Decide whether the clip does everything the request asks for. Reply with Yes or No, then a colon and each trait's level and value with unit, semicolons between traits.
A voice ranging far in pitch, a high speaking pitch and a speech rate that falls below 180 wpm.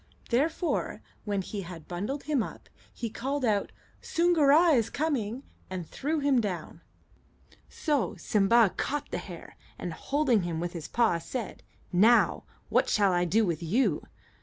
Yes: wide, 7.1 semitones; high, 230 Hz; average, 150 wpm